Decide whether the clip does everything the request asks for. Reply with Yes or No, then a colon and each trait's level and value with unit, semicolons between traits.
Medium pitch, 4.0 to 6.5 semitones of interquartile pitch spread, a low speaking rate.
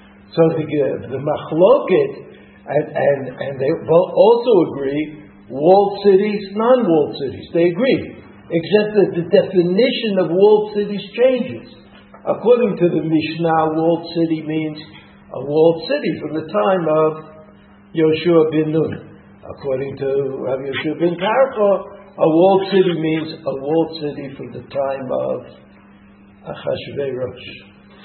Yes: medium, 165 Hz; wide, 5.4 semitones; slow, 125 wpm